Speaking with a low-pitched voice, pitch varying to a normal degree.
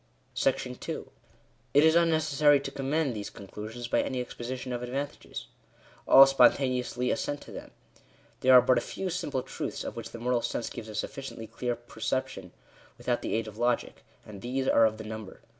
Yes: low, 125 Hz; average, 3.2 semitones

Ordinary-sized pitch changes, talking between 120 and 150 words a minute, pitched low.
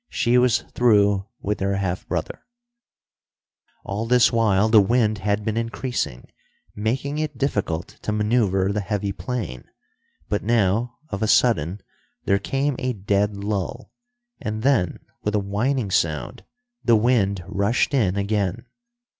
Yes: average, 3.2 semitones; average, 140 wpm; low, 105 Hz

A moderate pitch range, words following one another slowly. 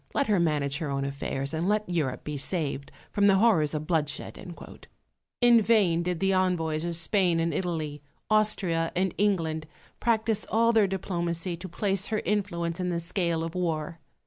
No: average, 3.7 semitones; average, 170 wpm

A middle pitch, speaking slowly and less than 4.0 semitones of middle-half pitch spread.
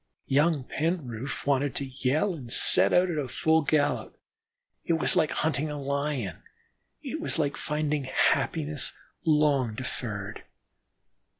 Yes: medium, 145 Hz; slow, 125 wpm; average, 3.0 semitones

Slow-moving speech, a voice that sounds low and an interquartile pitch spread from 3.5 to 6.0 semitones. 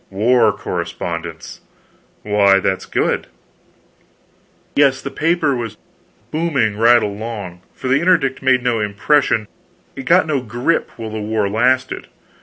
Yes: slow, 120 wpm; low, 120 Hz; average, 4.6 semitones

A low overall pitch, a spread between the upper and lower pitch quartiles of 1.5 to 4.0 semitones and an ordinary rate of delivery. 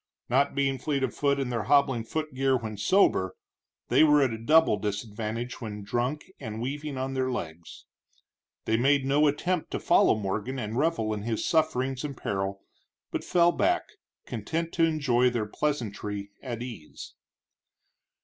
No: low, 130 Hz; average, 5.0 semitones; average, 160 wpm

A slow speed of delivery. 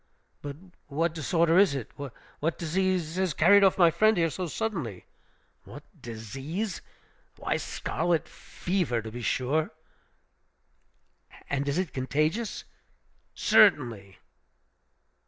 Yes: slow, 110 wpm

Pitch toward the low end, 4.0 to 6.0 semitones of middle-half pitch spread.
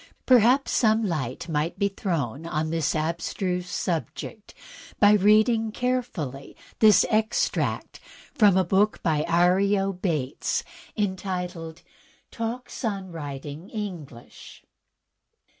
No: medium, 185 Hz; average, 4.7 semitones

